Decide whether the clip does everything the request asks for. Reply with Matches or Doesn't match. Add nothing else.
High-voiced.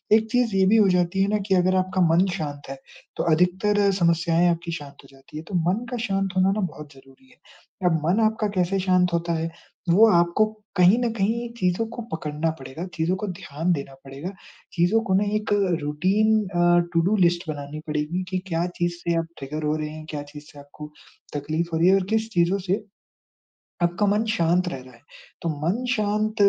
Doesn't match